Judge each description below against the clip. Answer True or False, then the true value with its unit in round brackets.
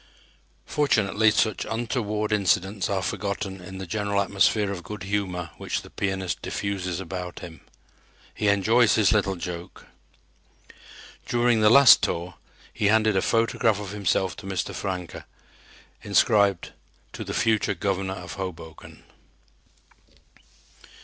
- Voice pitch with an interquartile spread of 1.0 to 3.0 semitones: True (2.4 semitones)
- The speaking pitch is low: True (100 Hz)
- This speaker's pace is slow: True (125 wpm)